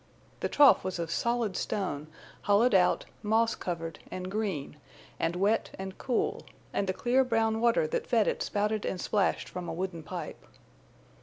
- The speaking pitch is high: Yes, high, 200 Hz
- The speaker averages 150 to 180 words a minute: Yes, average, 165 wpm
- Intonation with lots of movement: No, average, 3.9 semitones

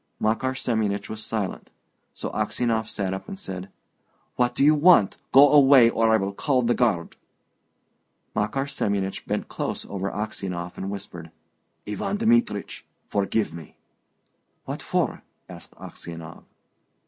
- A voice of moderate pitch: No, low, 110 Hz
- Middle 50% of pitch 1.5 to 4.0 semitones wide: No, average, 5.0 semitones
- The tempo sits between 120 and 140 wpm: Yes, slow, 135 wpm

